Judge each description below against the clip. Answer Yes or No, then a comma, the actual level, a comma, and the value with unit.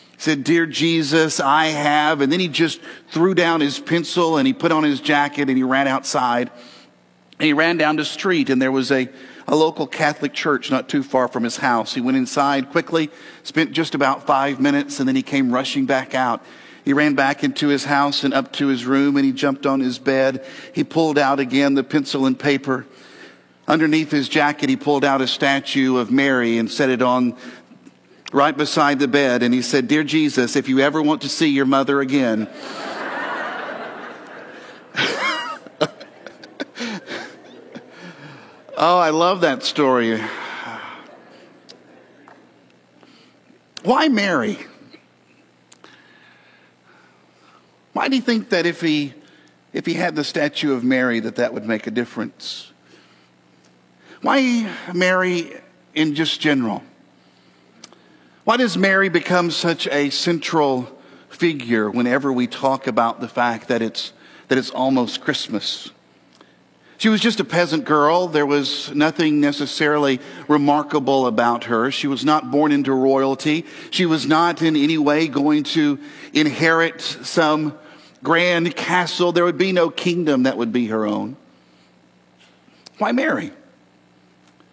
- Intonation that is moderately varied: Yes, average, 3.6 semitones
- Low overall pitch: No, medium, 145 Hz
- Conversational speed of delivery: Yes, average, 150 wpm